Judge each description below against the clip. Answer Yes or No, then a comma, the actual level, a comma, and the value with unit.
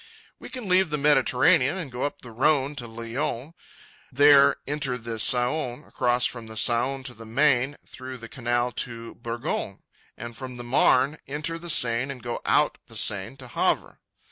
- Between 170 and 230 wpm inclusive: Yes, average, 175 wpm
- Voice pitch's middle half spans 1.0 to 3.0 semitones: No, average, 3.4 semitones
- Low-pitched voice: Yes, low, 125 Hz